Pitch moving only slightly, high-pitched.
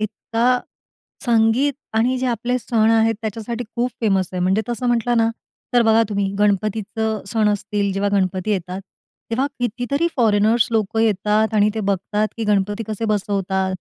Yes: narrow, 2.3 semitones; high, 220 Hz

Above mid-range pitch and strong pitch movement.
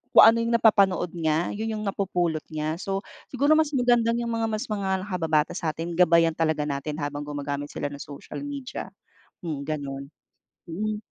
No: medium, 175 Hz; wide, 6.3 semitones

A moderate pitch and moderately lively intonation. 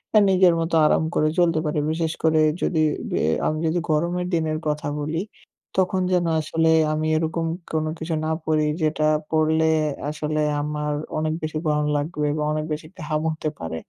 No: medium, 155 Hz; narrow, 1.1 semitones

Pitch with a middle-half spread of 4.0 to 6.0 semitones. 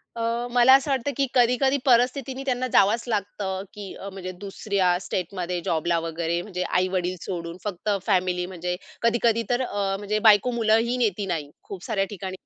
Yes: average, 4.6 semitones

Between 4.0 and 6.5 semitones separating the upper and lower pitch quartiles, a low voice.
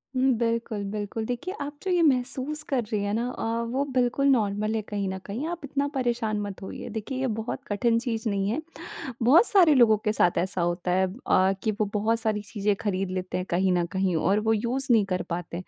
No: average, 4.4 semitones; high, 220 Hz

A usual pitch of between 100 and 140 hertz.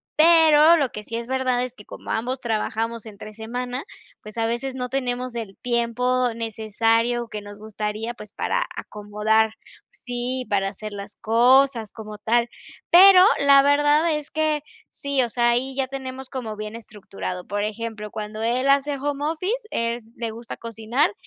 No: high, 235 Hz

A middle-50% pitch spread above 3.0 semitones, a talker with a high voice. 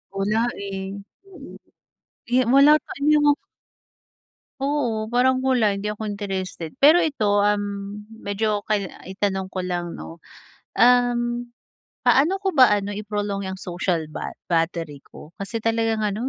Yes: average, 4.0 semitones; high, 210 Hz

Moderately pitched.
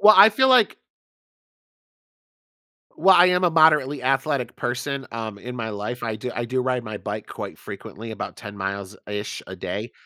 No: low, 125 Hz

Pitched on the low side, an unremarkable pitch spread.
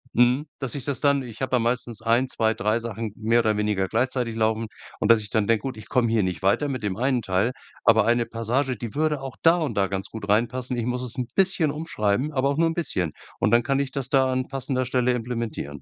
Yes: low, 120 Hz; average, 3.2 semitones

